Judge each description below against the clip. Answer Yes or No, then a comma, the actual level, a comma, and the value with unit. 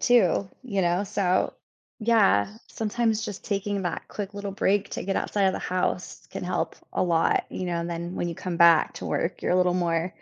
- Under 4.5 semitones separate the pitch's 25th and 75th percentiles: Yes, average, 2.8 semitones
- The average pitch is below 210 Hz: Yes, medium, 185 Hz